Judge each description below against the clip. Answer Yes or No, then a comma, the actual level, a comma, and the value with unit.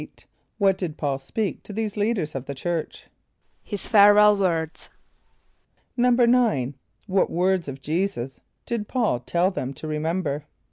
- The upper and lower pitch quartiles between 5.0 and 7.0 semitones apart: Yes, wide, 5.6 semitones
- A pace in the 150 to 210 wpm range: No, average, 140 wpm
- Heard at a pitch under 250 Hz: Yes, medium, 185 Hz